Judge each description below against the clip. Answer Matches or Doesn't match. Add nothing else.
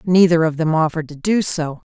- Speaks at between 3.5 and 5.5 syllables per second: Doesn't match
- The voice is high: Doesn't match